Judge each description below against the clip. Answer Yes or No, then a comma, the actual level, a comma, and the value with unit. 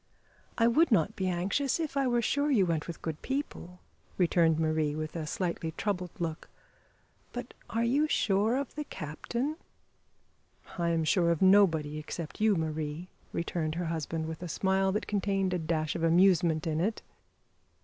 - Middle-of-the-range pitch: Yes, medium, 180 Hz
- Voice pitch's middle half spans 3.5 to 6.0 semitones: Yes, average, 5.1 semitones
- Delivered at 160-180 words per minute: Yes, average, 170 wpm